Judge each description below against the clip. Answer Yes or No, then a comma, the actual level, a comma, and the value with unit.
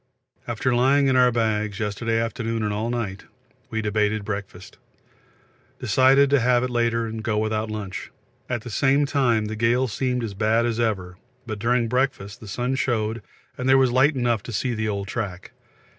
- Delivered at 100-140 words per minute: No, average, 180 wpm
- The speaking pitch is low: Yes, low, 115 Hz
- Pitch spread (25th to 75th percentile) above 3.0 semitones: No, average, 2.7 semitones